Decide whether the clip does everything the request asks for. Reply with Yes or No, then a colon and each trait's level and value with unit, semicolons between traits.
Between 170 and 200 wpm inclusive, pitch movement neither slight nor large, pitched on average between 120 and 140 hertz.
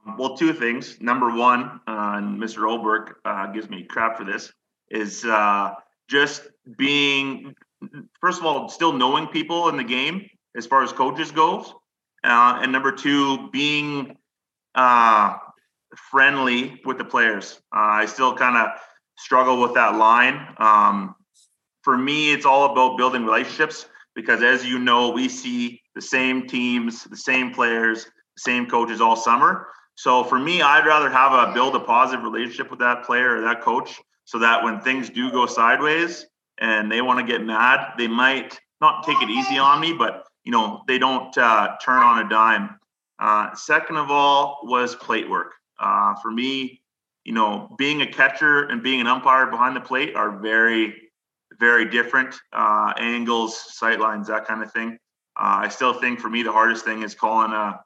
Yes: average, 175 wpm; average, 3.4 semitones; low, 125 Hz